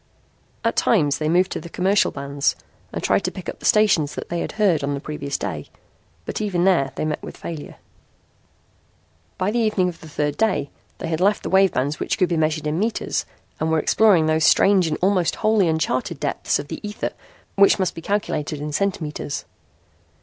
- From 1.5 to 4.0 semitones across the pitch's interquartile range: No, average, 4.5 semitones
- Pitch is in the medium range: Yes, medium, 165 Hz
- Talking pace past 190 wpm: Yes, average, 200 wpm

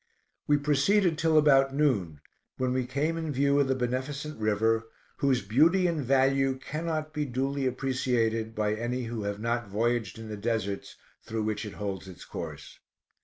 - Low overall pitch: Yes, low, 130 Hz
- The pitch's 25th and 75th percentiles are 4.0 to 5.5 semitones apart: Yes, average, 4.3 semitones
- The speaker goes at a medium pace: Yes, average, 170 wpm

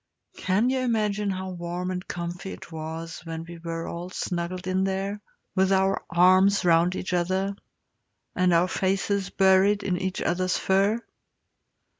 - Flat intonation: Yes, narrow, 2.0 semitones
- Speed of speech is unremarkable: Yes, average, 150 wpm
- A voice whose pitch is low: No, medium, 185 Hz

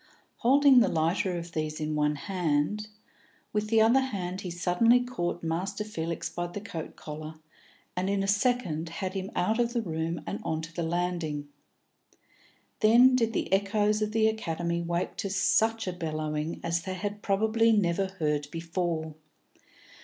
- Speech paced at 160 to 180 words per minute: Yes, average, 165 wpm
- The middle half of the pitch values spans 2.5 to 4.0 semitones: No, average, 4.5 semitones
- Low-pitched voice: No, medium, 180 Hz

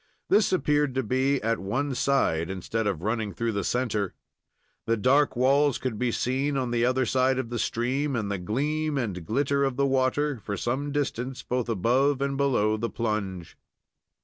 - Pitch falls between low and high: No, low, 125 Hz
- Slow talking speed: No, average, 180 wpm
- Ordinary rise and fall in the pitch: Yes, average, 4.2 semitones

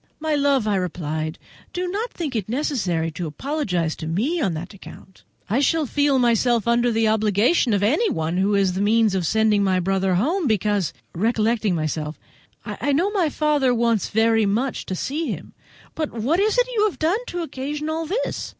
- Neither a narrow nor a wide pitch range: No, wide, 7.7 semitones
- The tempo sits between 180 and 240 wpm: Yes, average, 185 wpm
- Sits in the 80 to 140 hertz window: No, high, 225 Hz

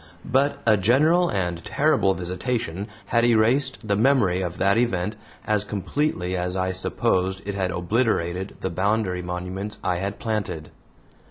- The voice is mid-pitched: No, low, 100 Hz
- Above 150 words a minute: No, average, 145 wpm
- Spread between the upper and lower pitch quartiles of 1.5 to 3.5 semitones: No, average, 4.2 semitones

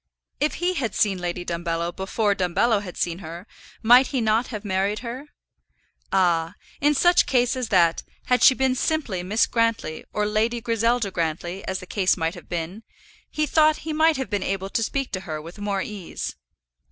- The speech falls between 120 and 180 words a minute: No, average, 190 wpm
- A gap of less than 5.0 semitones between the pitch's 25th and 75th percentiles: No, wide, 5.6 semitones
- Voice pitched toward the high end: Yes, high, 205 Hz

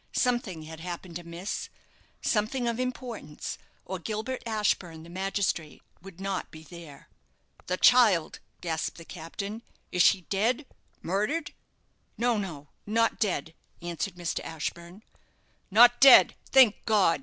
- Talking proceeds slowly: Yes, slow, 125 wpm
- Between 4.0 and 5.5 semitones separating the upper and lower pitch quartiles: Yes, average, 5.0 semitones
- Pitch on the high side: Yes, high, 195 Hz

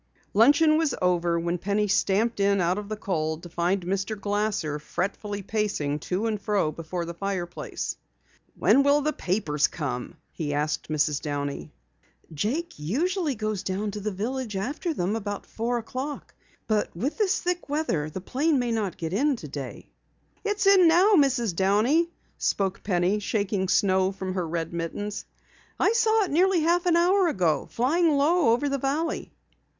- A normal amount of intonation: No, wide, 8.2 semitones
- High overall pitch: Yes, high, 205 Hz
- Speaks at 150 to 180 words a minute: Yes, average, 165 wpm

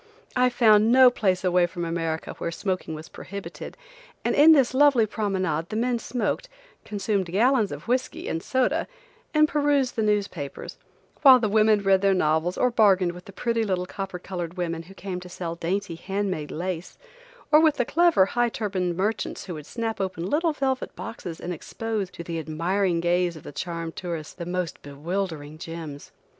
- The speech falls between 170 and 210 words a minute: Yes, average, 180 wpm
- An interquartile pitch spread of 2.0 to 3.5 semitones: No, average, 5.1 semitones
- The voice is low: No, high, 190 Hz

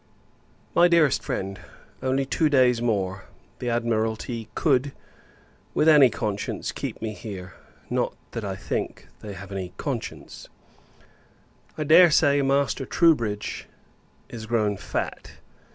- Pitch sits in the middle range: No, low, 120 Hz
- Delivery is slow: Yes, slow, 125 wpm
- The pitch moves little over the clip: No, wide, 5.4 semitones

